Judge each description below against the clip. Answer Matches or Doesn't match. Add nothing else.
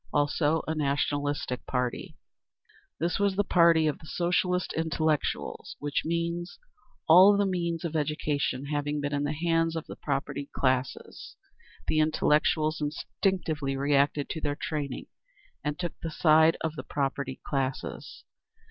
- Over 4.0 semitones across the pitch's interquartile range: Doesn't match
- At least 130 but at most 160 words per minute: Matches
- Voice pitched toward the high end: Doesn't match